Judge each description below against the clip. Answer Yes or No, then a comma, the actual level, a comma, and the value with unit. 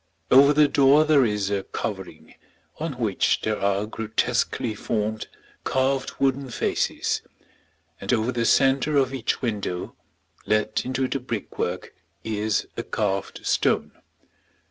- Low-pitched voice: Yes, low, 115 Hz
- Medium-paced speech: No, slow, 125 wpm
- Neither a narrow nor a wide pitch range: Yes, average, 4.2 semitones